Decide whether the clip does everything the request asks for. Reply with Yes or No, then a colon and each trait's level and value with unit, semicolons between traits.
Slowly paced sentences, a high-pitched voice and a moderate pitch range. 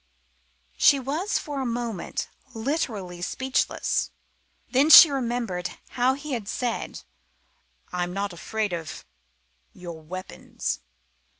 No: slow, 110 wpm; high, 230 Hz; wide, 6.7 semitones